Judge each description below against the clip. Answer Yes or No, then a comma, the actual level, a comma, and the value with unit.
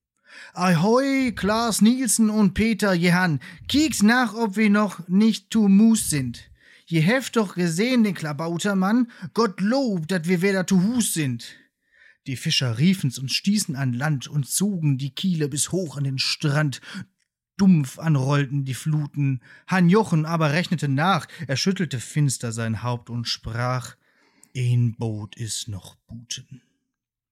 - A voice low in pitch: No, medium, 165 Hz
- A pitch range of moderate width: No, wide, 7.3 semitones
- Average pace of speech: Yes, average, 145 wpm